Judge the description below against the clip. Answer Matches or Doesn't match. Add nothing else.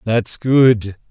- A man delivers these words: Matches